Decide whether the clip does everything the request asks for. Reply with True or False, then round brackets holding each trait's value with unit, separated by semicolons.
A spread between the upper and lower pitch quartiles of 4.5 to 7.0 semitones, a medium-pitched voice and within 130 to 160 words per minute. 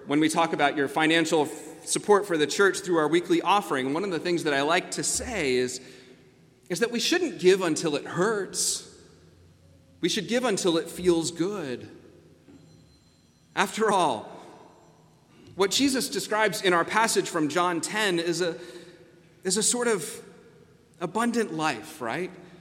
True (4.8 semitones; 170 Hz; 155 wpm)